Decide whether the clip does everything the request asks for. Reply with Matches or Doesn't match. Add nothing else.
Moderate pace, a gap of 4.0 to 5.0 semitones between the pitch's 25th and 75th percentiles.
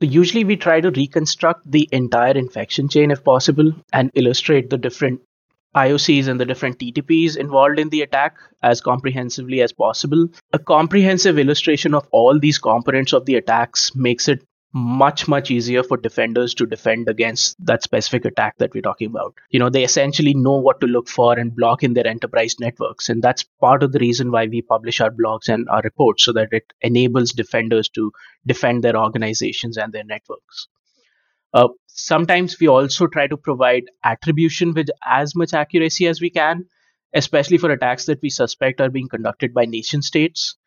Matches